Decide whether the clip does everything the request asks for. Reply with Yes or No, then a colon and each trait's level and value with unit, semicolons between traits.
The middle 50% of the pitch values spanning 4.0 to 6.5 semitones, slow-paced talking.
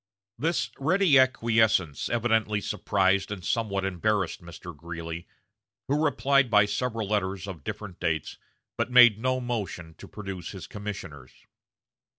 Yes: average, 4.4 semitones; slow, 130 wpm